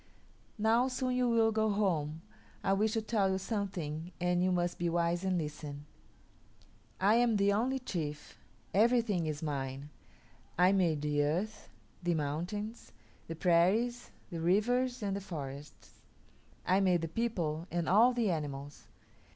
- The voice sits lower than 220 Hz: Yes, medium, 185 Hz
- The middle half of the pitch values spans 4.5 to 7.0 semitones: Yes, wide, 5.4 semitones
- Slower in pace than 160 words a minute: Yes, average, 150 wpm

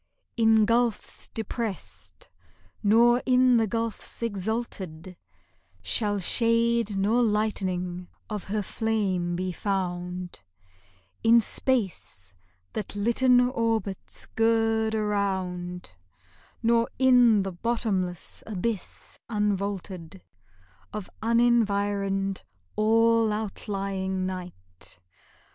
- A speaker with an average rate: No, slow, 80 wpm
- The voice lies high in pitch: Yes, high, 210 Hz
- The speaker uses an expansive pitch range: No, average, 3.5 semitones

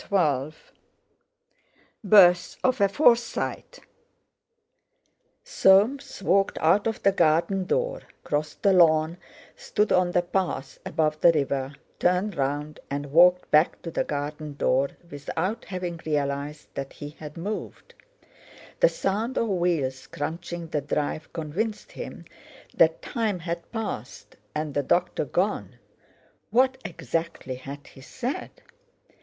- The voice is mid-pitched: Yes, medium, 170 Hz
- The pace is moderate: No, slow, 125 wpm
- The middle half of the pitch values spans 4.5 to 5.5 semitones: Yes, average, 5.0 semitones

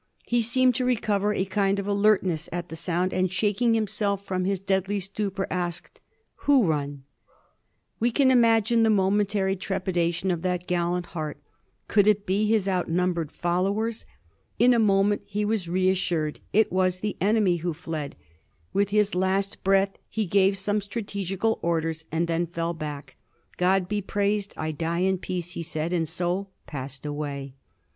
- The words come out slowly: No, average, 170 wpm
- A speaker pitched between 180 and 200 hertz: Yes, high, 190 Hz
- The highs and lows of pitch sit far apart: No, average, 3.0 semitones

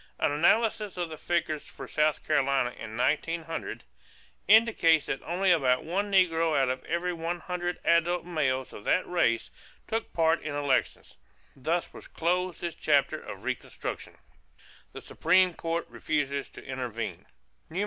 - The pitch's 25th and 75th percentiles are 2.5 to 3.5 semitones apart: No, average, 3.9 semitones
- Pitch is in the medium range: Yes, medium, 165 Hz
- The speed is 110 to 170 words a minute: Yes, average, 140 wpm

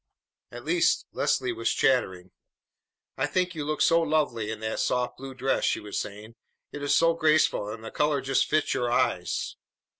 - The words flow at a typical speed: Yes, average, 180 wpm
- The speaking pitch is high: No, low, 135 Hz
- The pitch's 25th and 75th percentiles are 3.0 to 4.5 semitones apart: No, wide, 5.5 semitones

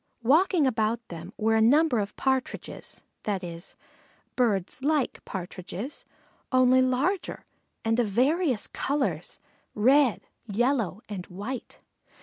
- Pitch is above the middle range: Yes, high, 240 Hz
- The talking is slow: Yes, slow, 115 wpm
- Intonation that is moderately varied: Yes, average, 4.7 semitones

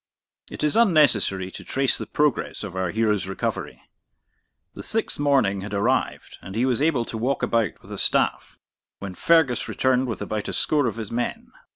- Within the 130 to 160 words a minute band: No, average, 185 wpm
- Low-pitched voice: Yes, low, 115 Hz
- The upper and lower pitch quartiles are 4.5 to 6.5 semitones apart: Yes, wide, 5.4 semitones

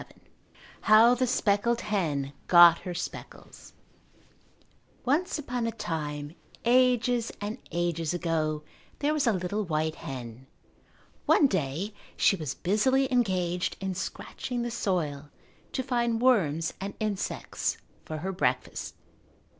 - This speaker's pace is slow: Yes, slow, 120 wpm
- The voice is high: Yes, high, 195 Hz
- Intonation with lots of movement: Yes, wide, 6.9 semitones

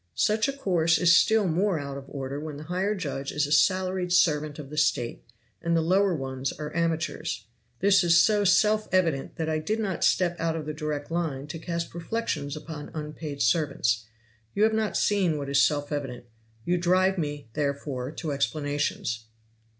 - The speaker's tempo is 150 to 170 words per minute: No, average, 185 wpm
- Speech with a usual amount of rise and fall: Yes, average, 4.2 semitones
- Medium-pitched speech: Yes, medium, 160 Hz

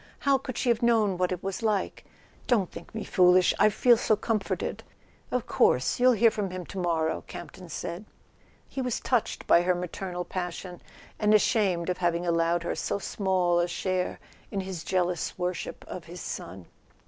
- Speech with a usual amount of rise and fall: Yes, average, 3.5 semitones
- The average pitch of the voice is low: No, medium, 185 Hz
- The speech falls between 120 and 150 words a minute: No, average, 180 wpm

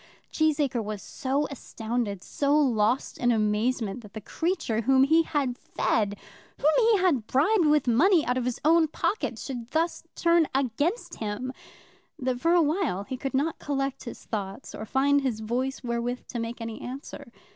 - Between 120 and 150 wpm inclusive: No, average, 170 wpm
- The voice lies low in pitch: No, very high, 260 Hz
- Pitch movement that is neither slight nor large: Yes, average, 4.7 semitones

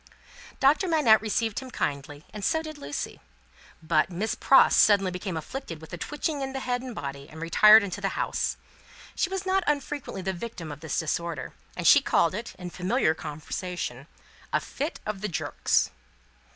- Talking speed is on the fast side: No, average, 180 wpm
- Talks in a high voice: Yes, high, 200 Hz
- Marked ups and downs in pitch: Yes, wide, 8.6 semitones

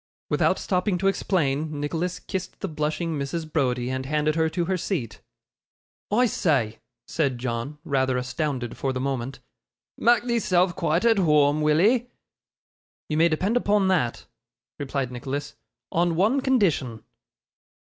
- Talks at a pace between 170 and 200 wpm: No, average, 140 wpm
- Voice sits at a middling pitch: Yes, medium, 155 Hz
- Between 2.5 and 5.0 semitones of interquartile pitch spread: No, wide, 5.4 semitones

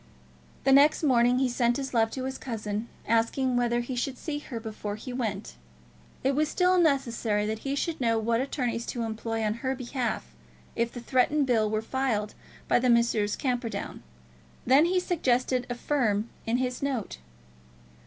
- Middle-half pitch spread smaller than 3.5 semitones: Yes, average, 3.0 semitones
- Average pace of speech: Yes, average, 170 wpm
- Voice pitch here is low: No, high, 245 Hz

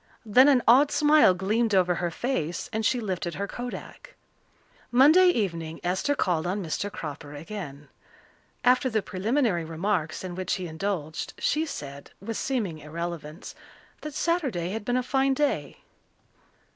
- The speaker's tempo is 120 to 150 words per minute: Yes, average, 145 wpm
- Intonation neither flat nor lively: No, wide, 6.9 semitones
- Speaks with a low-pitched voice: No, high, 200 Hz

